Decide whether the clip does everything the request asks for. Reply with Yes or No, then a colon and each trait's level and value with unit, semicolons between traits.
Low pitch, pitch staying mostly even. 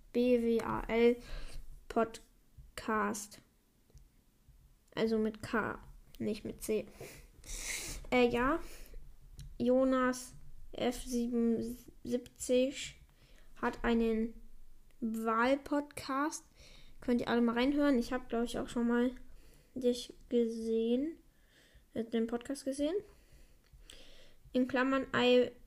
No: high, 245 Hz; narrow, 2.0 semitones